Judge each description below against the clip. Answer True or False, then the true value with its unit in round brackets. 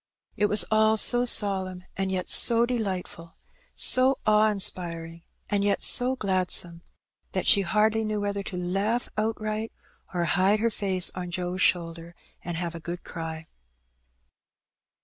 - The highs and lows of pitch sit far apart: False (3.4 semitones)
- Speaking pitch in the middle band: False (195 Hz)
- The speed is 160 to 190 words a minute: False (145 wpm)